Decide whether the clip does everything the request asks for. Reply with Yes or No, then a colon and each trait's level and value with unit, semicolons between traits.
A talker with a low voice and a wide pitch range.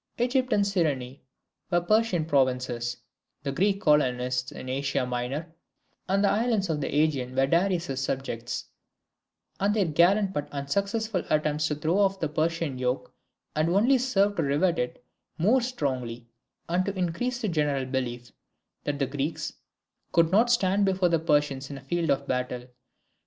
No: medium, 155 Hz; wide, 6.4 semitones